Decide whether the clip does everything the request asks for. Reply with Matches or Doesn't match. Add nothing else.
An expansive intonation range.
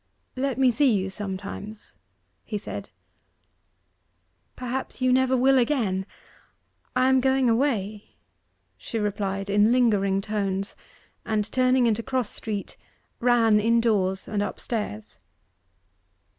Doesn't match